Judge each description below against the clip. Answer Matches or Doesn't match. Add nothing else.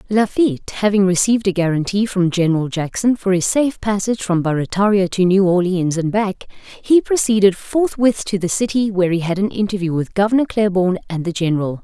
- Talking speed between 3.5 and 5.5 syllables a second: Doesn't match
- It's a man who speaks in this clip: Doesn't match